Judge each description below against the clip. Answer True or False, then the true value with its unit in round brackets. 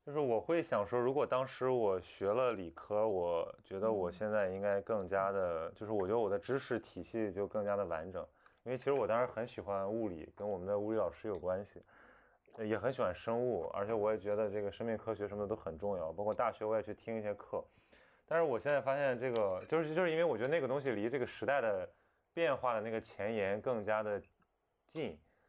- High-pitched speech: False (110 Hz)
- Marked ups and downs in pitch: False (3.7 semitones)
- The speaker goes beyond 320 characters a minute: True (330 characters per minute)